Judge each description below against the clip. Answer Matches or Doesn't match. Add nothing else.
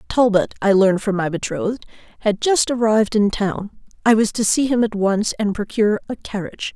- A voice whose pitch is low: Doesn't match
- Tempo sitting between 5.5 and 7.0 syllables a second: Matches